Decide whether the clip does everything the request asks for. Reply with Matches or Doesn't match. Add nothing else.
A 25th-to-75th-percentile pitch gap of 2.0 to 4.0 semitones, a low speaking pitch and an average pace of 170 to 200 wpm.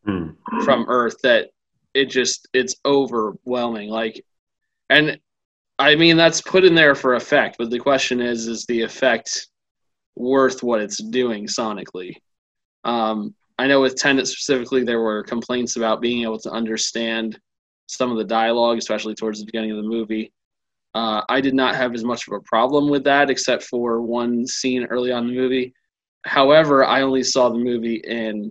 Matches